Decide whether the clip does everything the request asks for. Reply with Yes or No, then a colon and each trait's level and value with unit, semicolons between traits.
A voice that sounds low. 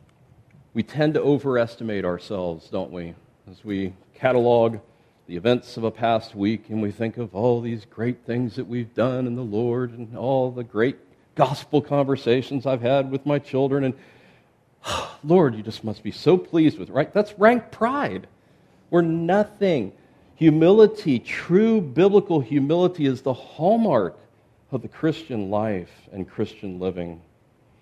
Yes: low, 125 Hz